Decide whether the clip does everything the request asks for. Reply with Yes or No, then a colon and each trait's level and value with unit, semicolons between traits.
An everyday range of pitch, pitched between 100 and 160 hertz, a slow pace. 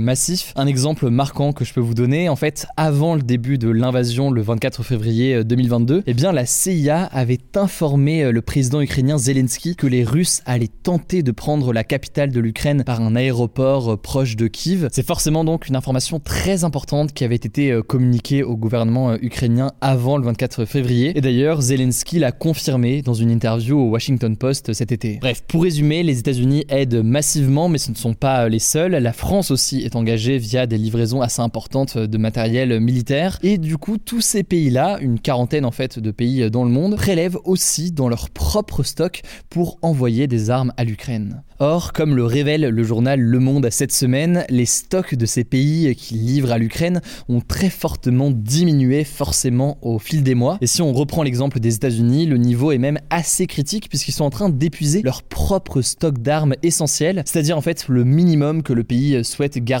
No: average, 4.0 semitones; low, 135 Hz; average, 195 wpm